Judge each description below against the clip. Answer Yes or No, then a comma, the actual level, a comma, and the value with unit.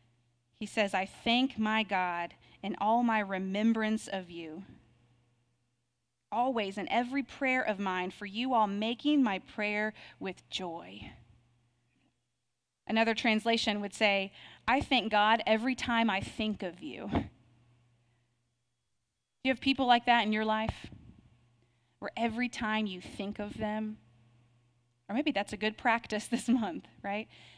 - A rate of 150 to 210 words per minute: No, average, 140 wpm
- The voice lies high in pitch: Yes, high, 200 Hz